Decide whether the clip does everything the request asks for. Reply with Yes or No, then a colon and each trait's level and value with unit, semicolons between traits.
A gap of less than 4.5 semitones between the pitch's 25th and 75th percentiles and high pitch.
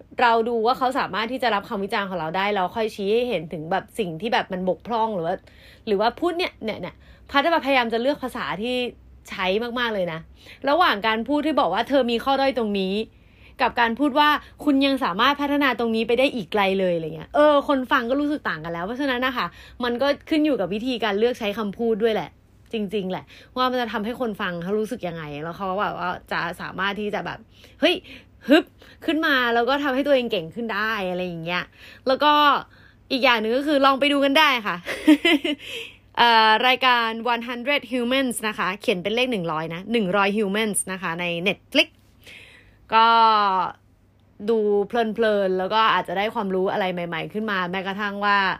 No: average, 4.8 semitones; high, 230 Hz